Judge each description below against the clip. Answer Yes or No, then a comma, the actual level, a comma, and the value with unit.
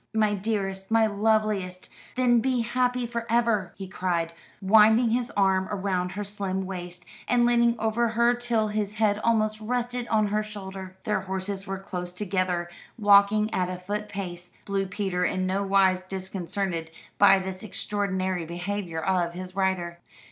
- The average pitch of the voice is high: Yes, high, 200 Hz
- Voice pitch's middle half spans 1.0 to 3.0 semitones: Yes, average, 2.7 semitones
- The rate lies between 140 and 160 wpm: Yes, average, 155 wpm